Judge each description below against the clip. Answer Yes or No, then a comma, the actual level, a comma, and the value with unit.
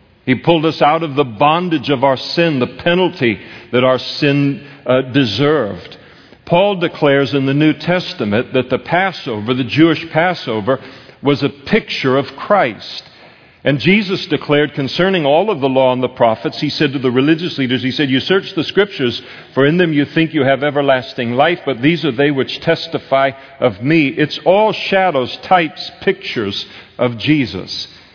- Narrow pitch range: No, average, 4.1 semitones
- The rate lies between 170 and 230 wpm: Yes, average, 175 wpm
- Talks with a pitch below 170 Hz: Yes, medium, 140 Hz